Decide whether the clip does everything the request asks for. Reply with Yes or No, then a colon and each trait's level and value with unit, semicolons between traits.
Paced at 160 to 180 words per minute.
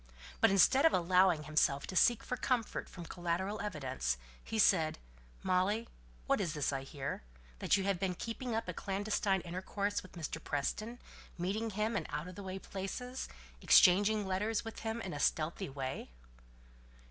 Yes: average, 170 wpm